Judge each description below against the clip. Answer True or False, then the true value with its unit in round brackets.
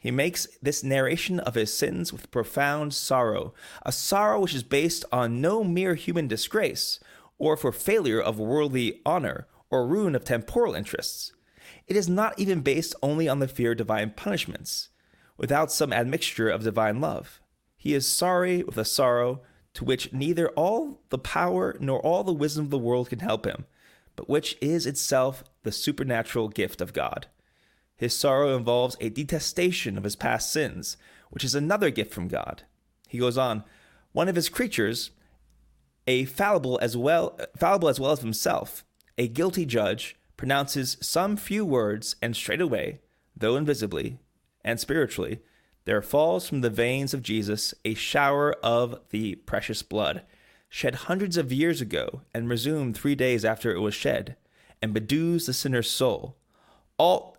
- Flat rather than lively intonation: False (5.1 semitones)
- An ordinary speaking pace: True (165 wpm)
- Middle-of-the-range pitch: False (130 Hz)